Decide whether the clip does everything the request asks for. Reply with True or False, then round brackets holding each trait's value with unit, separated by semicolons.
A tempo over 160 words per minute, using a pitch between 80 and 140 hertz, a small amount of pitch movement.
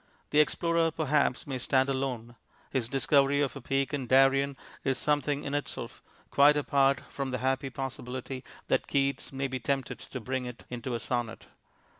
True (170 wpm; 135 Hz; 1.6 semitones)